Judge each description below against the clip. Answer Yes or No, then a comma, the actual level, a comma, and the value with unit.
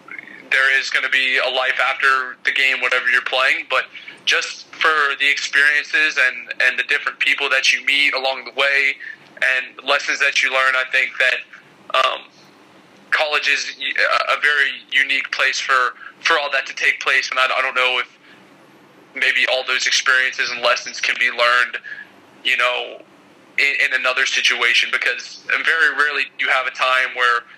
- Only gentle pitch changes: Yes, narrow, 1.0 semitones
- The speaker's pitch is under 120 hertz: No, low, 130 Hz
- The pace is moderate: Yes, average, 175 wpm